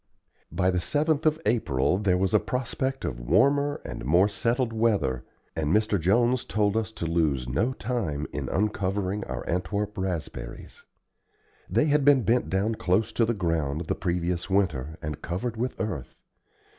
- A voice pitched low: Yes, low, 100 Hz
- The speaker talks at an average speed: Yes, average, 160 wpm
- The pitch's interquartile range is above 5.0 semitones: Yes, wide, 5.6 semitones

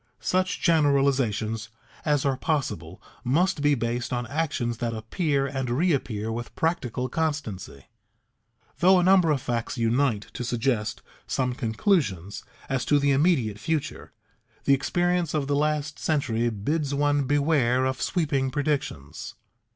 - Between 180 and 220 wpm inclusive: No, slow, 135 wpm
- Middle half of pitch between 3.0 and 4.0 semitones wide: No, average, 4.4 semitones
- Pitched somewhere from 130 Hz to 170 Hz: Yes, low, 135 Hz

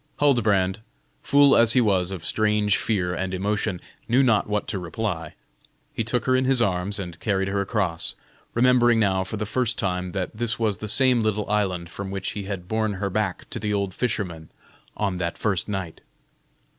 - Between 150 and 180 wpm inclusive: No, average, 190 wpm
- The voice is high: No, low, 105 Hz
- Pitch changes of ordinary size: Yes, average, 3.1 semitones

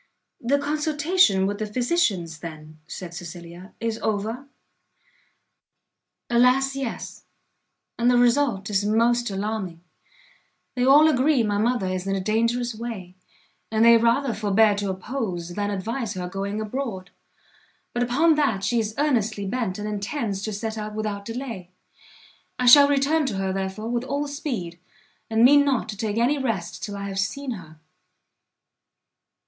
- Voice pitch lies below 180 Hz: No, high, 220 Hz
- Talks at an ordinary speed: Yes, average, 150 wpm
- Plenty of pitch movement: No, average, 4.4 semitones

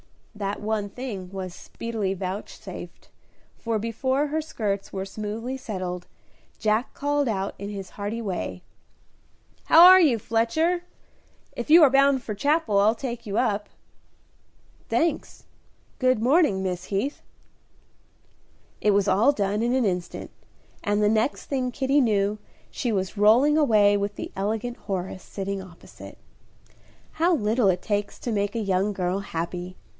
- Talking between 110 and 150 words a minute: Yes, average, 145 wpm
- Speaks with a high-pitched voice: Yes, high, 215 Hz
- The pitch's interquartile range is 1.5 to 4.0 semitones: No, average, 4.5 semitones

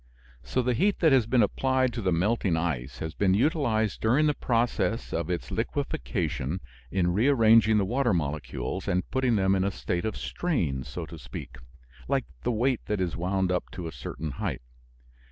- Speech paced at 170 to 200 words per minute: Yes, average, 185 wpm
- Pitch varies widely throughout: Yes, wide, 5.9 semitones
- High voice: No, low, 105 Hz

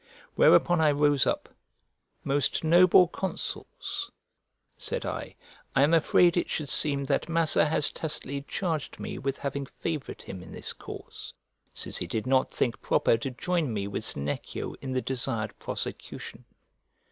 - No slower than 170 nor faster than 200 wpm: No, average, 150 wpm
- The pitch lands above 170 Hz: No, medium, 140 Hz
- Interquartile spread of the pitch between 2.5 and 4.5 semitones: Yes, average, 4.0 semitones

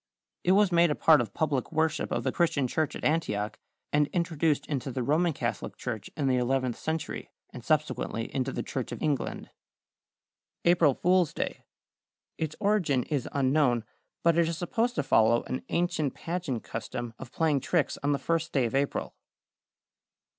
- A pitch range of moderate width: Yes, average, 4.5 semitones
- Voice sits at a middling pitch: Yes, medium, 150 Hz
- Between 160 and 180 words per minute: Yes, average, 170 wpm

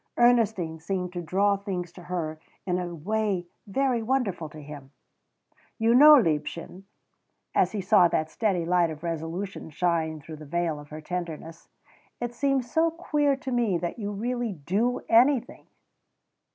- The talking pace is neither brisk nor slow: Yes, average, 155 wpm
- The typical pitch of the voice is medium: Yes, medium, 180 Hz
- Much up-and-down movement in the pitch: Yes, wide, 6.1 semitones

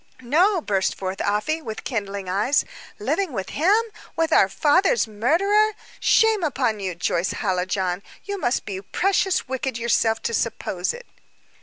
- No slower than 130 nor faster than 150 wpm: Yes, average, 145 wpm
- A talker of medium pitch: No, high, 235 Hz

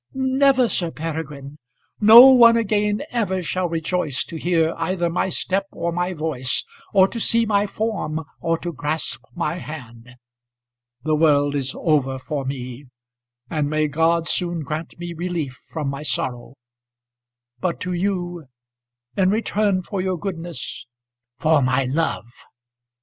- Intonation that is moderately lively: Yes, average, 4.4 semitones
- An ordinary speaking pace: Yes, average, 145 wpm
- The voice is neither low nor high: Yes, medium, 165 Hz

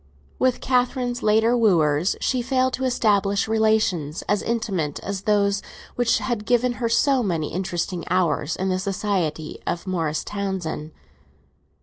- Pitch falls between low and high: No, high, 200 Hz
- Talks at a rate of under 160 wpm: Yes, slow, 135 wpm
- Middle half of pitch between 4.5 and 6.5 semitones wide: Yes, average, 5.2 semitones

